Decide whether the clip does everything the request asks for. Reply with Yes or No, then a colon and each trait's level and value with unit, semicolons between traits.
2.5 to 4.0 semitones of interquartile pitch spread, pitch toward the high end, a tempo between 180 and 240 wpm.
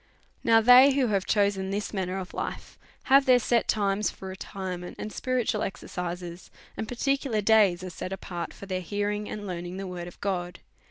Yes: average, 3.2 semitones; high, 200 Hz; average, 200 wpm